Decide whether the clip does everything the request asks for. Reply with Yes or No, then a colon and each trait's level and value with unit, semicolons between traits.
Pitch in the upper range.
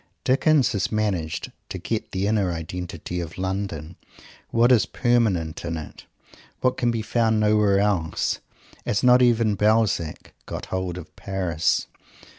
No: low, 100 Hz